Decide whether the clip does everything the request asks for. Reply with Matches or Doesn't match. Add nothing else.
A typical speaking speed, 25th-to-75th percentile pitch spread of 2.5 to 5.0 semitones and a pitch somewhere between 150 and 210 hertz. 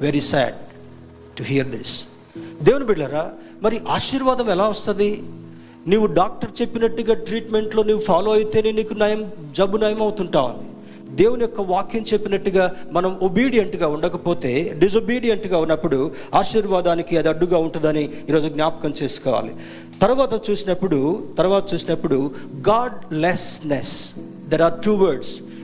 Doesn't match